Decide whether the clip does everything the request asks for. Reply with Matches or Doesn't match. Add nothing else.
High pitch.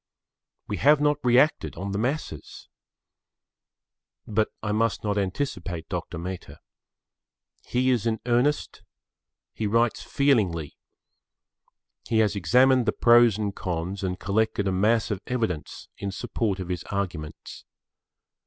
Doesn't match